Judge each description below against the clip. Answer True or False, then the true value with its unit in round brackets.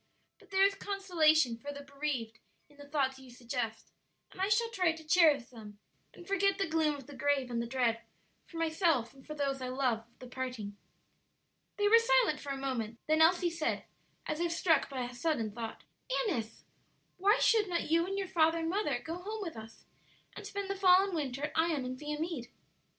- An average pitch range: False (5.9 semitones)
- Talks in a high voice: True (300 Hz)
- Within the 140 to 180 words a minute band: False (205 wpm)